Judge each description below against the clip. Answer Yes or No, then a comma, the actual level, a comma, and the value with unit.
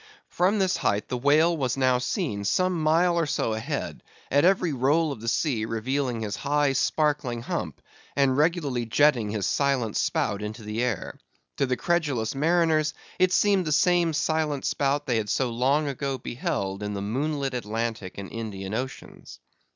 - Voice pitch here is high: No, low, 135 Hz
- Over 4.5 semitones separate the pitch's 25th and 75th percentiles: Yes, average, 5.3 semitones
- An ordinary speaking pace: Yes, average, 170 wpm